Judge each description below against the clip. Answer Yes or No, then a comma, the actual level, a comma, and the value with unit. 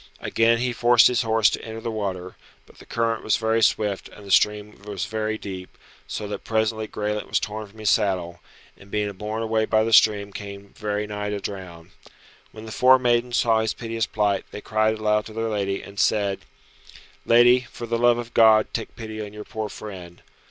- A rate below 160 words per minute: No, fast, 205 wpm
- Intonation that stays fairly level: Yes, narrow, 1.9 semitones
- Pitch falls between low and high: No, low, 110 Hz